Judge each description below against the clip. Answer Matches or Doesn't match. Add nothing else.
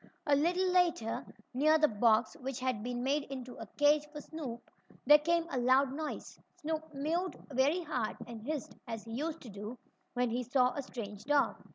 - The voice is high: Matches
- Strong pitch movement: Doesn't match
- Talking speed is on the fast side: Doesn't match